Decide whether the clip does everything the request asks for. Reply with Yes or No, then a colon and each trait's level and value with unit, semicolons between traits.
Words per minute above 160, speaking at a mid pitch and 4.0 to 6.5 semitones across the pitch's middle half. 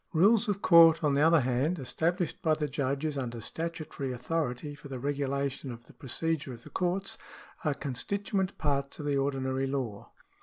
No: average, 175 wpm; medium, 145 Hz; average, 3.6 semitones